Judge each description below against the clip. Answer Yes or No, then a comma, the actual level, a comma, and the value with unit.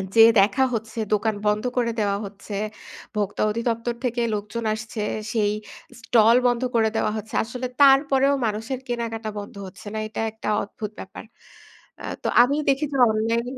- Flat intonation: Yes, narrow, 2.3 semitones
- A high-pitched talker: Yes, high, 225 Hz